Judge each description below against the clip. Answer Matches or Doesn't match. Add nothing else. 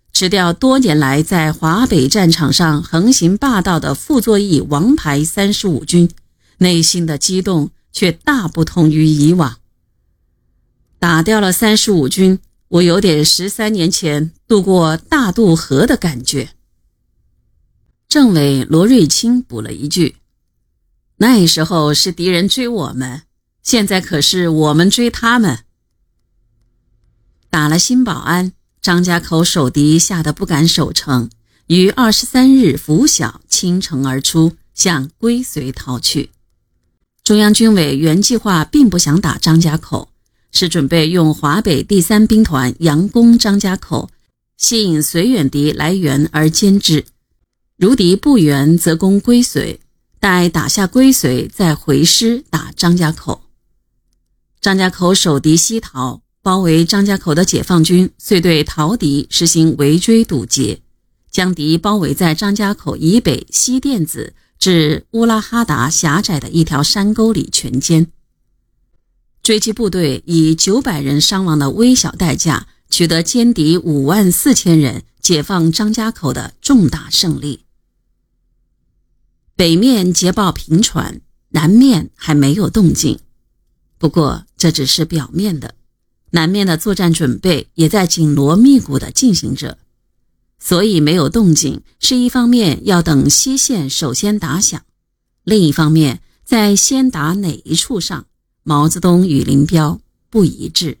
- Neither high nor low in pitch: Matches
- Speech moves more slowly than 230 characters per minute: Matches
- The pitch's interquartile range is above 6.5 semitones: Doesn't match